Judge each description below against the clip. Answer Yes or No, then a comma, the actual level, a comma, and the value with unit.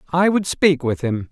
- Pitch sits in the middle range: Yes, medium, 150 Hz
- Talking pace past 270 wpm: No, fast, 230 wpm